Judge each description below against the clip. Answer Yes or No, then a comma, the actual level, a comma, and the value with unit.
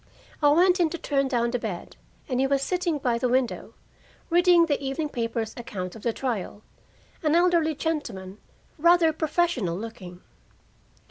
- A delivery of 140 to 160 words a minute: Yes, average, 155 wpm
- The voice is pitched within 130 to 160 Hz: No, very high, 270 Hz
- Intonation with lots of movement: Yes, wide, 6.2 semitones